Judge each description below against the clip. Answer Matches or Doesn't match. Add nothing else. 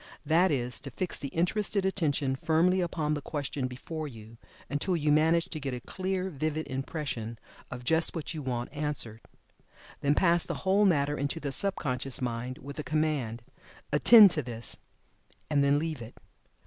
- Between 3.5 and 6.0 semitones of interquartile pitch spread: Matches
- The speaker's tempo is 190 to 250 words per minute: Doesn't match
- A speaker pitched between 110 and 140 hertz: Doesn't match